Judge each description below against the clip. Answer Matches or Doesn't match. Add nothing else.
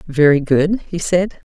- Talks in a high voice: Doesn't match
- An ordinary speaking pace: Matches